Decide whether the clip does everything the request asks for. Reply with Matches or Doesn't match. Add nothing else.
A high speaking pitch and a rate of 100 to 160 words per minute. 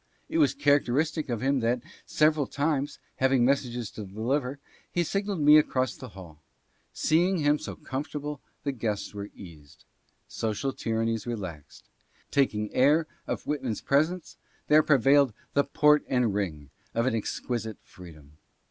Doesn't match